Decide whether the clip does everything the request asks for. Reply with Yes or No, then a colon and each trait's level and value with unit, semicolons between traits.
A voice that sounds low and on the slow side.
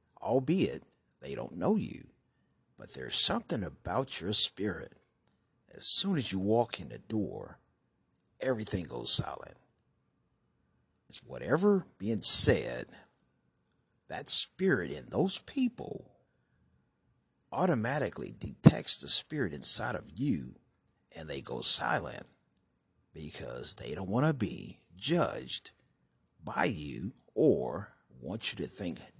Yes: low, 105 Hz; slow, 115 wpm